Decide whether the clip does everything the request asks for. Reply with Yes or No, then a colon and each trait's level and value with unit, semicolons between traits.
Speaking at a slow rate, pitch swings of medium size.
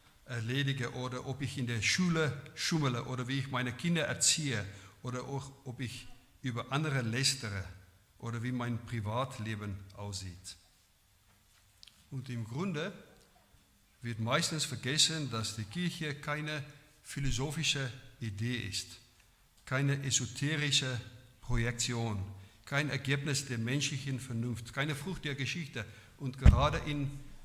Yes: slow, 120 wpm; average, 3.8 semitones